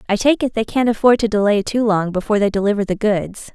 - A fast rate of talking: Yes, fast, 255 wpm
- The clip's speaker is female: Yes, female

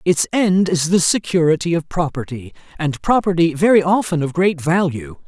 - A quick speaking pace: No, average, 160 wpm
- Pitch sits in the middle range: Yes, medium, 165 Hz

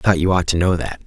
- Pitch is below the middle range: Yes, very low, 90 Hz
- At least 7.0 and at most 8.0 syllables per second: Yes, 7.5 syllables/s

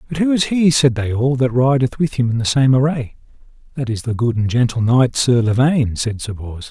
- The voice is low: Yes, low, 125 Hz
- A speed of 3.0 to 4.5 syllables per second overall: No, 5.4 syllables/s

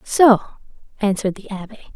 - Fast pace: No, slow, 125 wpm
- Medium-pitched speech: No, high, 210 Hz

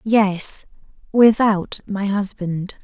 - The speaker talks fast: No, slow, 85 wpm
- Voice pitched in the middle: No, high, 200 Hz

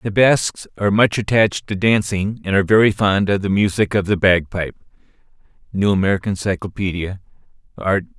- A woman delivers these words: No, male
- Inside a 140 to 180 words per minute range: Yes, average, 155 wpm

